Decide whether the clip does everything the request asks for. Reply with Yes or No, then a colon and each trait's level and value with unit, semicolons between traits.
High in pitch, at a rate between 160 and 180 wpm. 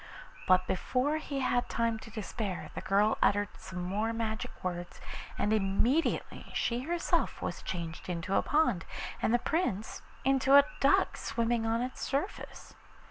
No: high, 225 Hz; average, 150 wpm